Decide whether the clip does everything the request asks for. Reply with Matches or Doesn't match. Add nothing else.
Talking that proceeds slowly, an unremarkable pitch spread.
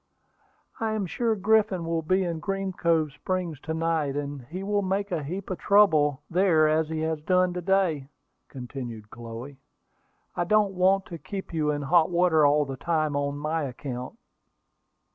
Doesn't match